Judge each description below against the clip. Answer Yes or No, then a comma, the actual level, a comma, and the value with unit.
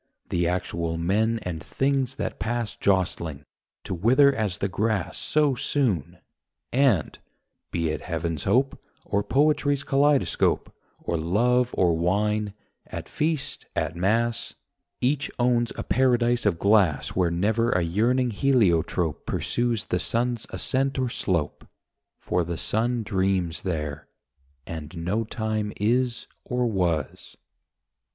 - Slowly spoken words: Yes, slow, 125 wpm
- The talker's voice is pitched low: Yes, low, 105 Hz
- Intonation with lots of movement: Yes, wide, 6.1 semitones